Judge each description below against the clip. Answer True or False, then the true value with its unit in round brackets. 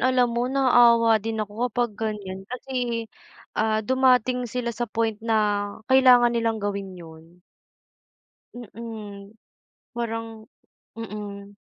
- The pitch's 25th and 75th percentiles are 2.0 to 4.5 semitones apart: True (2.8 semitones)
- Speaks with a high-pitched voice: True (225 Hz)